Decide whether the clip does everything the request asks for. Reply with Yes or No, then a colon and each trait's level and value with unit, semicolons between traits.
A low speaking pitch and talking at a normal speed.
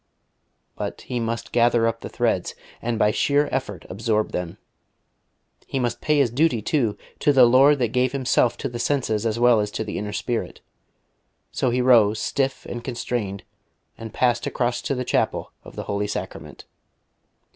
Yes: low, 120 Hz; average, 175 wpm